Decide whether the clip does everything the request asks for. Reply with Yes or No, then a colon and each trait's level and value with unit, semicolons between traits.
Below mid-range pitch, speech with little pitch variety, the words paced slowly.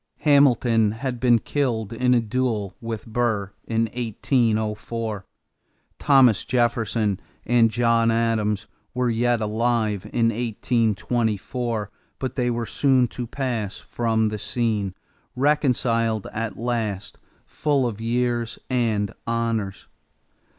Yes: low, 115 Hz; narrow, 2.0 semitones; slow, 110 wpm